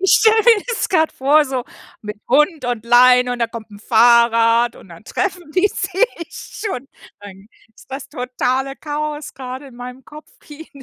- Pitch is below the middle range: No, very high, 265 Hz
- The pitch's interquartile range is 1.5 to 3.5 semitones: No, average, 4.8 semitones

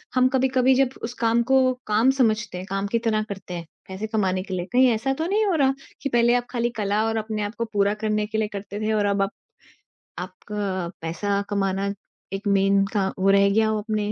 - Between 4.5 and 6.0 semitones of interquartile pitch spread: No, average, 2.8 semitones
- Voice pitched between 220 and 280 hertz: No, high, 210 Hz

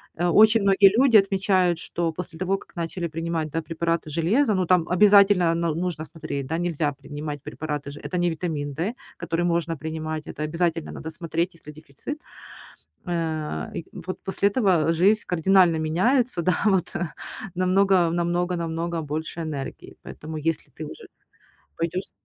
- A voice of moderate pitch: Yes, medium, 170 Hz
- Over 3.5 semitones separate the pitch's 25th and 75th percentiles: No, narrow, 2.6 semitones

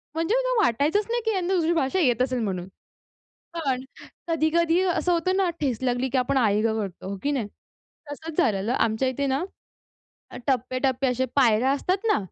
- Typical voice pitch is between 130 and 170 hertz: No, very high, 270 Hz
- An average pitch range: No, wide, 5.7 semitones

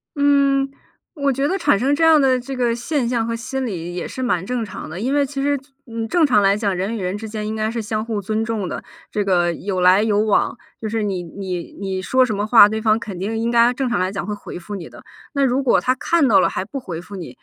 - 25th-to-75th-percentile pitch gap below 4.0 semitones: No, average, 4.6 semitones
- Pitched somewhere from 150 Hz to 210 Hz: No, high, 220 Hz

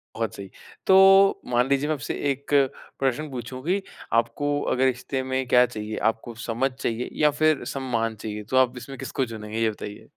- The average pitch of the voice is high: No, low, 130 Hz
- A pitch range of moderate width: Yes, average, 3.4 semitones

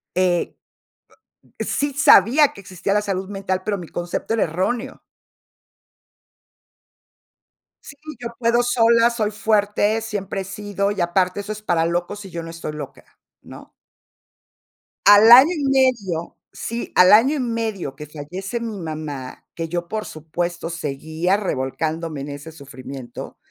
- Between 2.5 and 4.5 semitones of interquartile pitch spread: No, average, 5.1 semitones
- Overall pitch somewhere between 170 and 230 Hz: Yes, high, 190 Hz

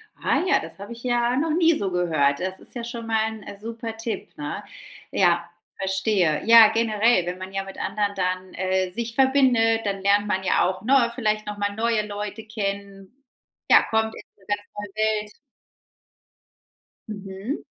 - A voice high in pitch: Yes, high, 210 Hz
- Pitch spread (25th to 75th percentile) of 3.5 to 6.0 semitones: No, average, 3.0 semitones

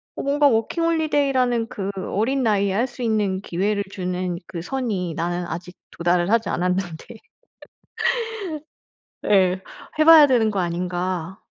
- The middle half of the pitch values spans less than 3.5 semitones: No, wide, 5.5 semitones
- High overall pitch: Yes, high, 195 Hz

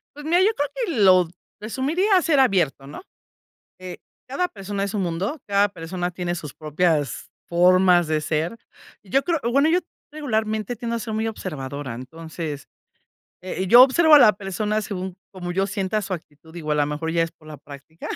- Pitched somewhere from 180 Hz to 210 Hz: Yes, medium, 185 Hz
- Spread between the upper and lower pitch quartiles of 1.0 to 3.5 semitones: No, wide, 5.6 semitones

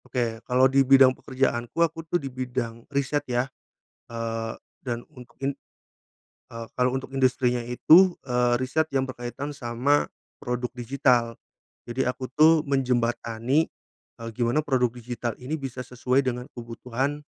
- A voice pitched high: No, low, 125 Hz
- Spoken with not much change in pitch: Yes, narrow, 2.1 semitones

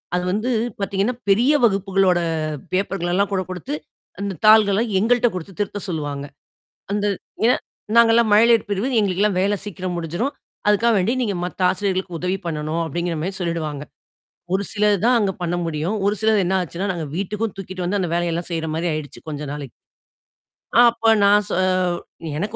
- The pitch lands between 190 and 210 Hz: Yes, high, 195 Hz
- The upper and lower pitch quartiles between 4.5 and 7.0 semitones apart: No, average, 3.3 semitones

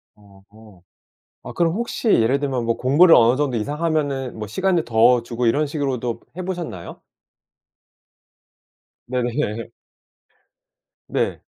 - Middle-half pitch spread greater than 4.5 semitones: Yes, average, 5.2 semitones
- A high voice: No, low, 125 Hz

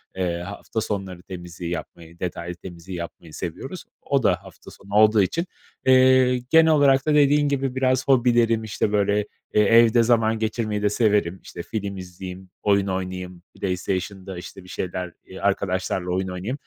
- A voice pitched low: Yes, low, 100 Hz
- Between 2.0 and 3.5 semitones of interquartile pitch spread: No, average, 4.2 semitones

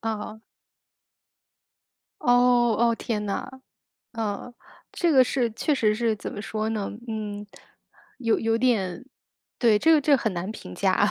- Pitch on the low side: No, high, 225 Hz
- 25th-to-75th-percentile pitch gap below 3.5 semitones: Yes, narrow, 2.6 semitones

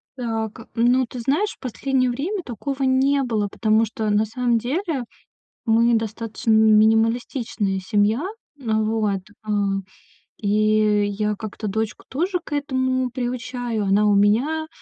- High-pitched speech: Yes, high, 230 Hz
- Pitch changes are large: No, average, 3.3 semitones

